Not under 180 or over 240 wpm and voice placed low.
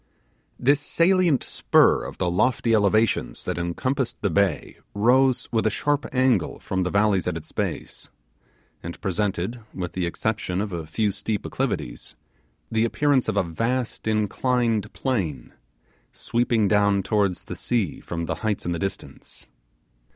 No: average, 150 wpm; low, 105 Hz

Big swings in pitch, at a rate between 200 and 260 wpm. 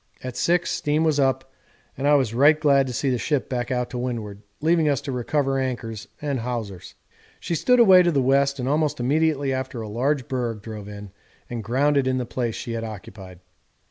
No: average, 3.7 semitones; fast, 205 wpm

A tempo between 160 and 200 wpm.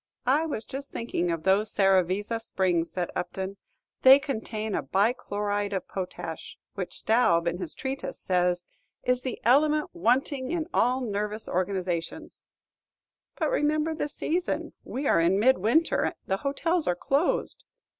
No: average, 145 wpm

